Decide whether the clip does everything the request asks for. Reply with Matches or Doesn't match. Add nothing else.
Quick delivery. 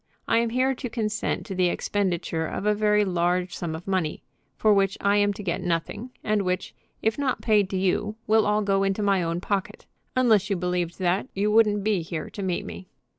Matches